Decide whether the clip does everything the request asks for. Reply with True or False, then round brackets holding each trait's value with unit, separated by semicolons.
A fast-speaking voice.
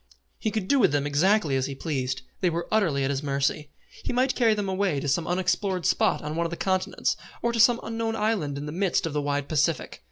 True (245 wpm)